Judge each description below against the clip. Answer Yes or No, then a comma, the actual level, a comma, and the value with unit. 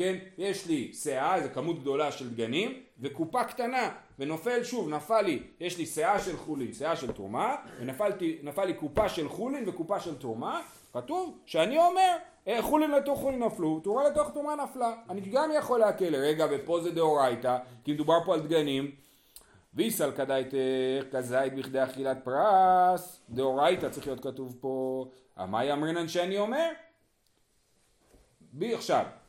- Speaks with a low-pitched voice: No, medium, 170 Hz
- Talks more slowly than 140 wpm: No, fast, 150 wpm